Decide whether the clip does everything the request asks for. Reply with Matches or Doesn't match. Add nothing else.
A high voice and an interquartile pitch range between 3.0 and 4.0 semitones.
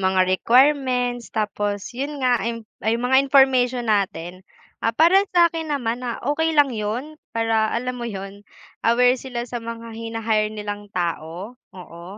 Matches